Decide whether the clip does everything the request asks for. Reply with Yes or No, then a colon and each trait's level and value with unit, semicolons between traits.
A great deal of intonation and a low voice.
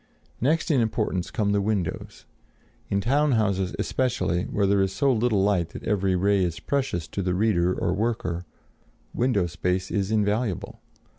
No: average, 3.7 semitones; low, 100 Hz